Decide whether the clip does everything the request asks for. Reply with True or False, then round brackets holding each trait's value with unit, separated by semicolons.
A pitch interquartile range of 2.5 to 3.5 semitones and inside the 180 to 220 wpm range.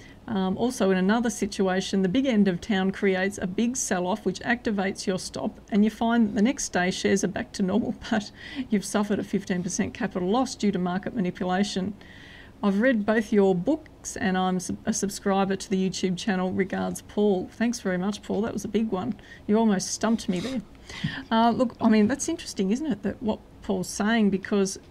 True (2.9 semitones; 200 wpm)